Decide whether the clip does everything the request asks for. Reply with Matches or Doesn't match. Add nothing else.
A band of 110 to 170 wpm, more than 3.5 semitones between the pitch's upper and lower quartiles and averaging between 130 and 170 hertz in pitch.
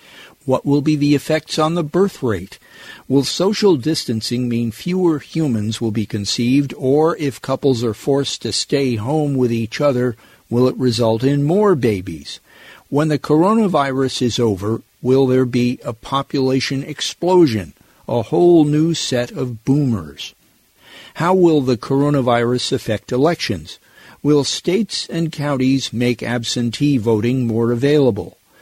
Matches